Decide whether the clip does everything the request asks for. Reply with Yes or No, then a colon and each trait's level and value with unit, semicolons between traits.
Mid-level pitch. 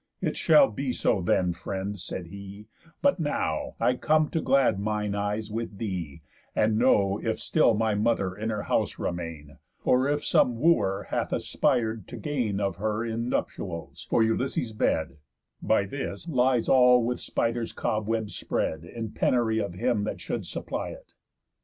No: low, 110 Hz